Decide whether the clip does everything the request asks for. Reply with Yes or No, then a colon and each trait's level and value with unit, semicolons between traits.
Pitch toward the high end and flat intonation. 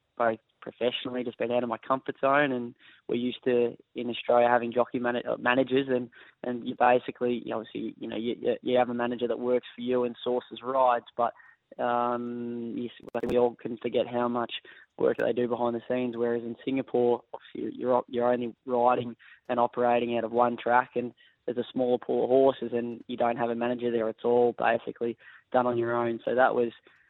No: low, 120 Hz; narrow, 0.7 semitones